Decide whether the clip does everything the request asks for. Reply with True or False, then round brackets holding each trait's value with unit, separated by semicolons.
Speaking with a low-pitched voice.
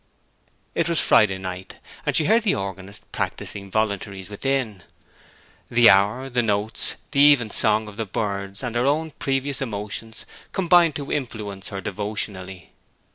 True (110 Hz)